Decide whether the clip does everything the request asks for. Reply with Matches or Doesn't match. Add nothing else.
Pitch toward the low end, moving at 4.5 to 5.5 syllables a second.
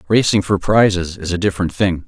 Doesn't match